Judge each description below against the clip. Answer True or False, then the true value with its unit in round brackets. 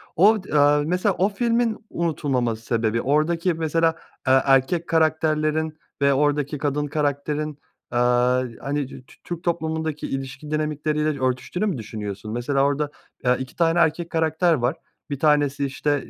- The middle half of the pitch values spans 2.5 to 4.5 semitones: True (3.2 semitones)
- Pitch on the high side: False (150 Hz)